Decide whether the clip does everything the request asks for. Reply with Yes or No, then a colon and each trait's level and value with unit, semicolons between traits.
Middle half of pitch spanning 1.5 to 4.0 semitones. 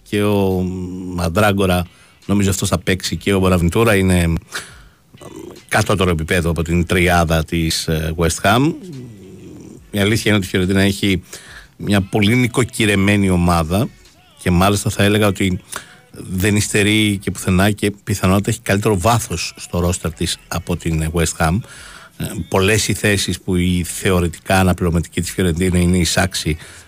Yes: average, 2.8 semitones